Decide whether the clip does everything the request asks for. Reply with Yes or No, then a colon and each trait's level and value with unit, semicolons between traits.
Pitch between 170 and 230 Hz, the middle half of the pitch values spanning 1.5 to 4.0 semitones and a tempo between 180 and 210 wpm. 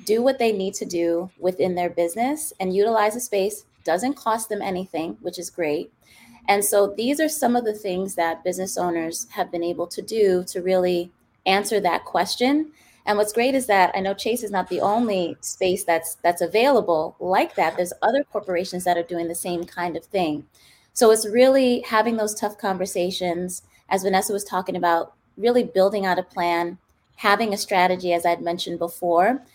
Yes: high, 190 Hz; average, 3.6 semitones; average, 190 wpm